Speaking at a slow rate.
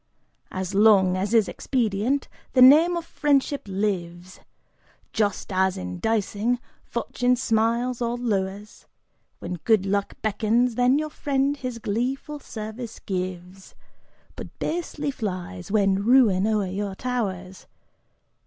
Yes: slow, 120 wpm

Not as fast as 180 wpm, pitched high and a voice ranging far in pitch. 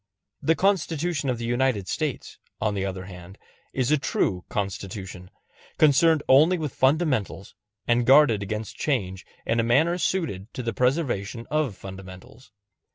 No: average, 145 wpm; low, 120 Hz; wide, 7.4 semitones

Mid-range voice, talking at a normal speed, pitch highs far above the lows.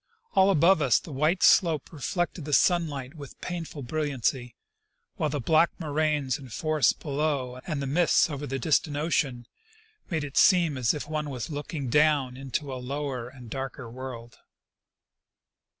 No: medium, 145 Hz; average, 155 wpm; average, 3.0 semitones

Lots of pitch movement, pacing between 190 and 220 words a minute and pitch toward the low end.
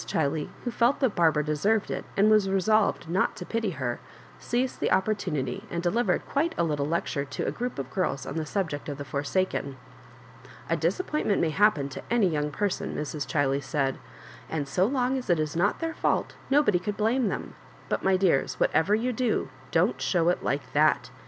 No: wide, 6.6 semitones; fast, 205 wpm; medium, 180 Hz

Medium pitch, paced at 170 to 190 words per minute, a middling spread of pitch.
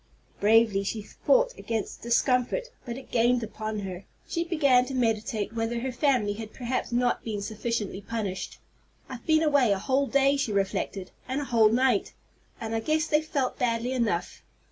No: high, 235 Hz; average, 175 wpm; average, 3.6 semitones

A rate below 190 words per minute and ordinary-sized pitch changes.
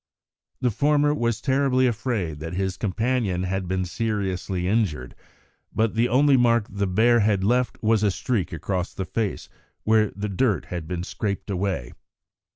Yes: average, 160 wpm; average, 4.2 semitones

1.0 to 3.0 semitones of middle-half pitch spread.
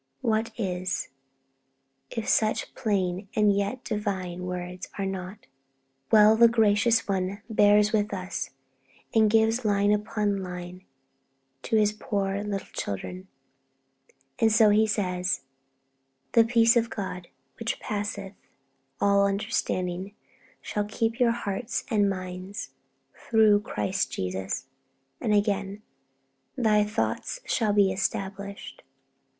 Yes: narrow, 2.4 semitones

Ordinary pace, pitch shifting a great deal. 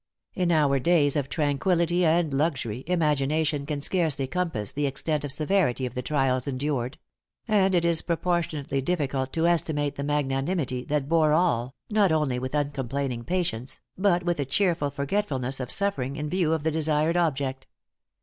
No: average, 160 wpm; average, 4.0 semitones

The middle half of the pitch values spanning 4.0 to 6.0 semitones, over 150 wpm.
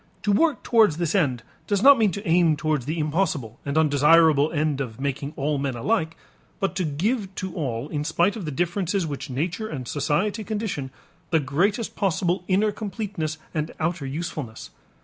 Yes: average, 5.3 semitones; average, 175 wpm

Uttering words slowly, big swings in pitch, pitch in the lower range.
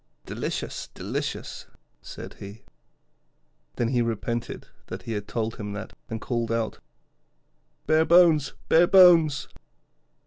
Yes: slow, 115 wpm; wide, 6.1 semitones; low, 120 Hz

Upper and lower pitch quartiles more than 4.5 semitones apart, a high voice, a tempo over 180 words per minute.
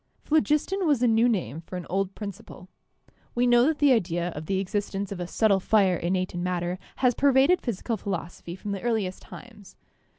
Yes: average, 4.9 semitones; high, 200 Hz; average, 195 wpm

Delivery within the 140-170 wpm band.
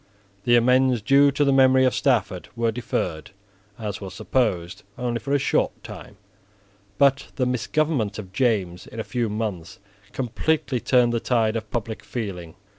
Yes: average, 160 wpm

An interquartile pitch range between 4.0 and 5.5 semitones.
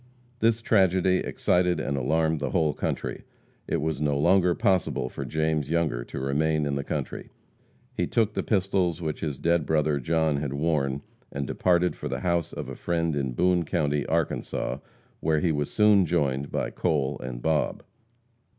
No: average, 3.5 semitones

